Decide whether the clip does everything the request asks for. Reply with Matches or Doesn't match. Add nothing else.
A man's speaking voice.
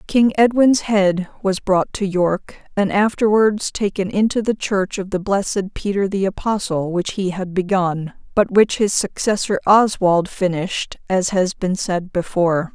Doesn't match